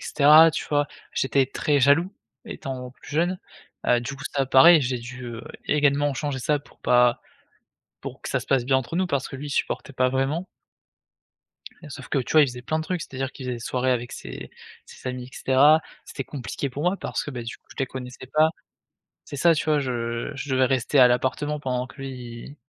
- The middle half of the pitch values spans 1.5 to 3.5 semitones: Yes, average, 2.8 semitones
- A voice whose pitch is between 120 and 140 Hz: Yes, low, 135 Hz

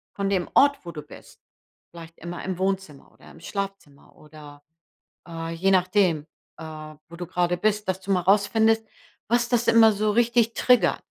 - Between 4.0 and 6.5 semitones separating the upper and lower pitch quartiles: Yes, average, 4.4 semitones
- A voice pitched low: No, high, 190 Hz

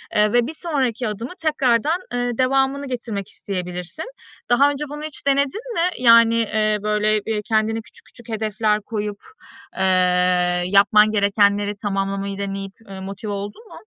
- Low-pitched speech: No, high, 215 Hz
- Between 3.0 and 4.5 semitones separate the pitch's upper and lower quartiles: Yes, average, 4.0 semitones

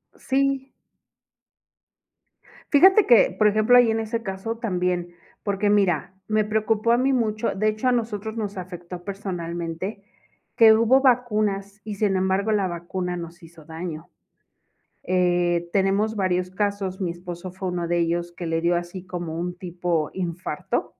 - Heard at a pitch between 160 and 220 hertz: Yes, high, 190 Hz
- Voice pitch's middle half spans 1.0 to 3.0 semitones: No, average, 3.7 semitones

